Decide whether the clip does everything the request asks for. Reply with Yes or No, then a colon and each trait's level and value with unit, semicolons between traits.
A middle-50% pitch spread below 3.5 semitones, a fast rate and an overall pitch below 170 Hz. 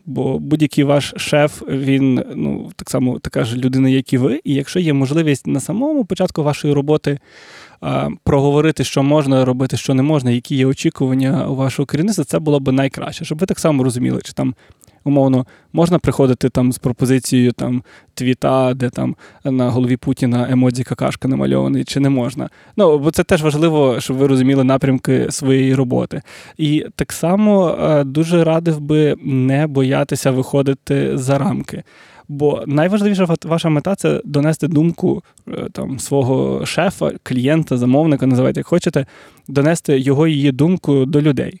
Yes: average, 2.8 semitones; fast, 160 wpm; medium, 140 Hz